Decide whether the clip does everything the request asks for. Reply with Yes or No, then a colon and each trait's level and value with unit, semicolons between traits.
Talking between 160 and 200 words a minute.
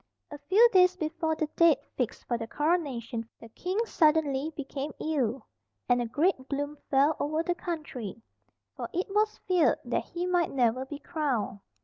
Yes: average, 165 wpm